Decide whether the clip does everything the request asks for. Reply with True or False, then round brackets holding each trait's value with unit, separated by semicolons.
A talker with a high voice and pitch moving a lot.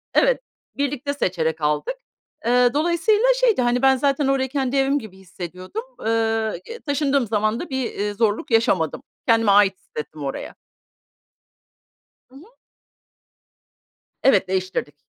True (245 Hz; 6.7 semitones)